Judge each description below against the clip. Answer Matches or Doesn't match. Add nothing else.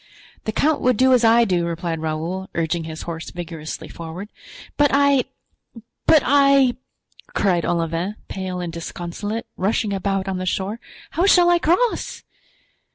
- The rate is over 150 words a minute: Doesn't match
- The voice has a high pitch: Matches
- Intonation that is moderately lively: Doesn't match